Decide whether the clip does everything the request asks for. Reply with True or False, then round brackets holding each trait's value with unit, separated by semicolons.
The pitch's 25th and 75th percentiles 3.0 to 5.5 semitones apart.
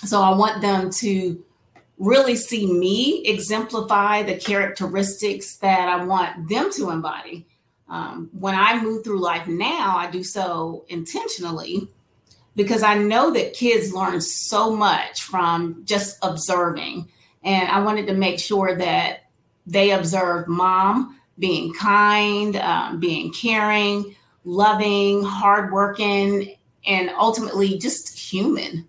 False (2.5 semitones)